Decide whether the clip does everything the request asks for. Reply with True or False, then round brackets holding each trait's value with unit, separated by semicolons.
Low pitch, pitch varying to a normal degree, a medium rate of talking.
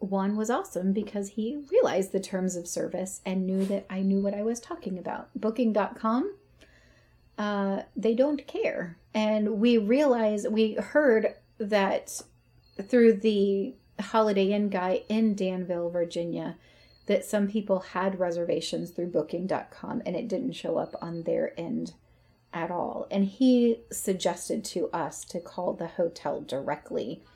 False (205 Hz; 3.1 semitones; 145 wpm)